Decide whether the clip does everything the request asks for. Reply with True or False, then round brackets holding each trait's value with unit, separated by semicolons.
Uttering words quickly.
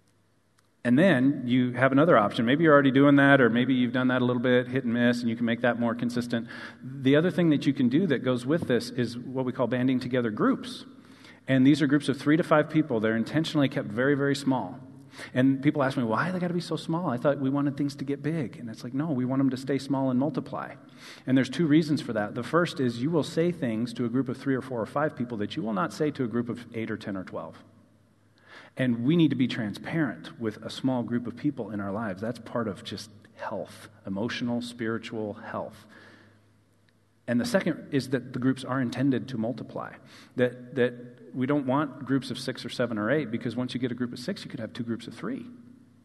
True (250 wpm)